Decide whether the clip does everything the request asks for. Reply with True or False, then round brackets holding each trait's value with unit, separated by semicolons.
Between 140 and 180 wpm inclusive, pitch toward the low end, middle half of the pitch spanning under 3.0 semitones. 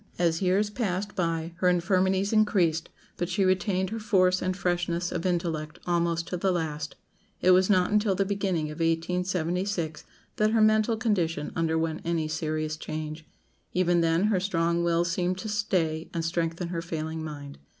False (165 wpm; 175 Hz; 2.5 semitones)